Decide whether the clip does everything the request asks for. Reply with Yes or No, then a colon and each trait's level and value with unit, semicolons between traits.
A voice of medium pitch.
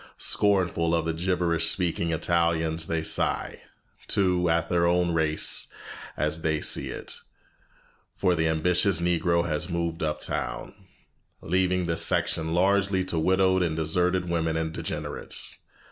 No: very low, 85 Hz